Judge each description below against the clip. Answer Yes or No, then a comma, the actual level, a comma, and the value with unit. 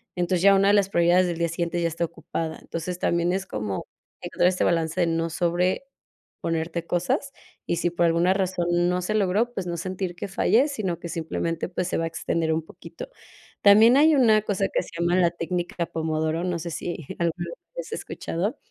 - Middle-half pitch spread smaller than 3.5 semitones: Yes, narrow, 2.4 semitones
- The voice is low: No, medium, 175 Hz